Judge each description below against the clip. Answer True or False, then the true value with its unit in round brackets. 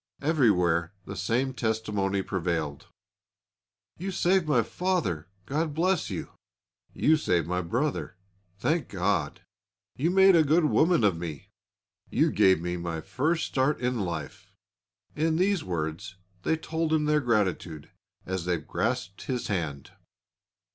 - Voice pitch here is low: True (110 Hz)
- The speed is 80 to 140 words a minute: True (135 wpm)